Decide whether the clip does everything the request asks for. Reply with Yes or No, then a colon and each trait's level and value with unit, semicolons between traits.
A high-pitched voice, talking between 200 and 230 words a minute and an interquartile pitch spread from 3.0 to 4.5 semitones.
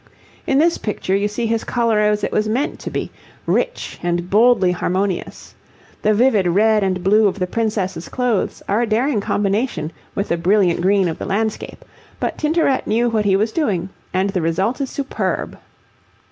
No: high, 210 Hz; average, 180 wpm; average, 3.4 semitones